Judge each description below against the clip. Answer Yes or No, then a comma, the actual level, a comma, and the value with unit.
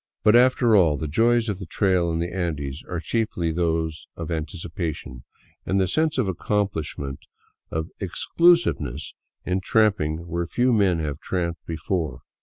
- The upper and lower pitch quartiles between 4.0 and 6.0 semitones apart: Yes, average, 4.5 semitones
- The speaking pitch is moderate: No, very low, 85 Hz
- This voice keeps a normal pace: Yes, average, 160 wpm